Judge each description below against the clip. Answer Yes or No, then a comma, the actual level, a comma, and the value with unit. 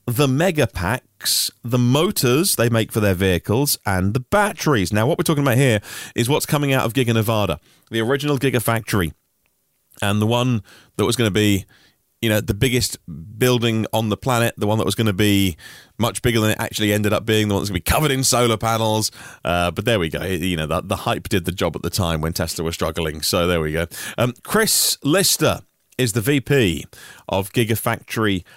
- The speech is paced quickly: Yes, fast, 215 wpm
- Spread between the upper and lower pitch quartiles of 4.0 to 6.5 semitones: Yes, average, 4.6 semitones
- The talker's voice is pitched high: No, low, 110 Hz